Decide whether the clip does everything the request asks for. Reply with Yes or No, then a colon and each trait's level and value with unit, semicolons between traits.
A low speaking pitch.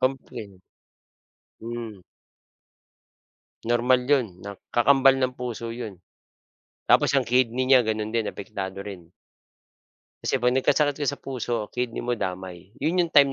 Yes: low, 120 Hz